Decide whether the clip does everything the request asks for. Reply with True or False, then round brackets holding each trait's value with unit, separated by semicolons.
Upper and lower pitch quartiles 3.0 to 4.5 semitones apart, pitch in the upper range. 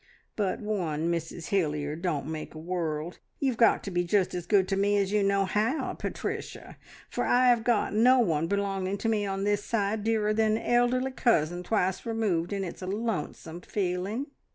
True (3.9 semitones; 200 Hz)